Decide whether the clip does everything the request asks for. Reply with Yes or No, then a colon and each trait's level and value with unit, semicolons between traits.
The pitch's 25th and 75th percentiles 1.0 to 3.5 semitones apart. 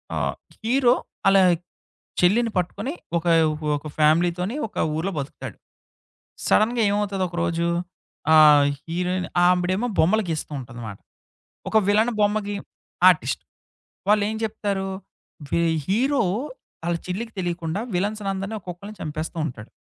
No: average, 4.0 semitones